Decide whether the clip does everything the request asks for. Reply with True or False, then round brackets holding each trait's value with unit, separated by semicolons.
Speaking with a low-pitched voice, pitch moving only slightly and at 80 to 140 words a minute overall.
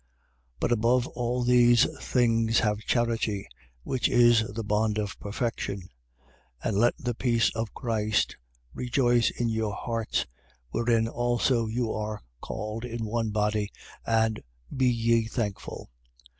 True (115 Hz; 2.0 semitones; 135 wpm)